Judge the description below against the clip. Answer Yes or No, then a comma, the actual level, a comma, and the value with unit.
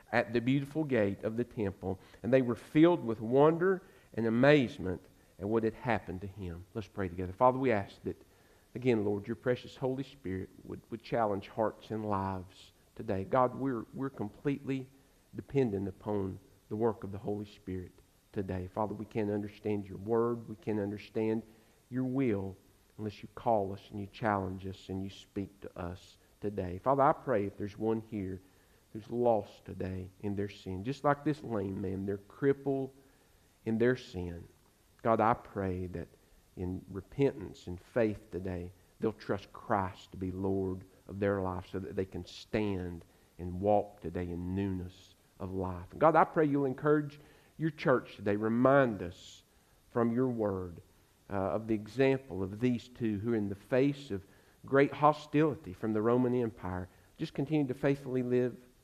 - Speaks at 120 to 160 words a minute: No, average, 175 wpm